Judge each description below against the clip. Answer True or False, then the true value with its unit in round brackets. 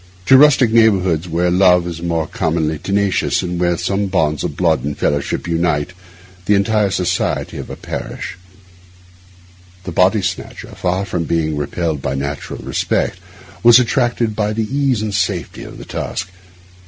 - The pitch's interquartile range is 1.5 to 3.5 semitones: False (4.2 semitones)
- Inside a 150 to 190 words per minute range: True (160 wpm)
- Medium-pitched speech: False (90 Hz)